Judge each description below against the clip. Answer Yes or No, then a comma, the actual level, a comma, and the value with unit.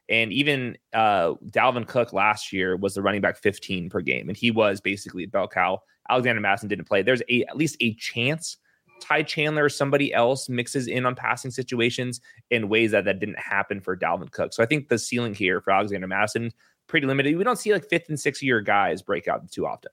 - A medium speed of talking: No, fast, 215 wpm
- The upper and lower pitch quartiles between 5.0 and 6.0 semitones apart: Yes, wide, 5.4 semitones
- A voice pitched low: Yes, low, 120 Hz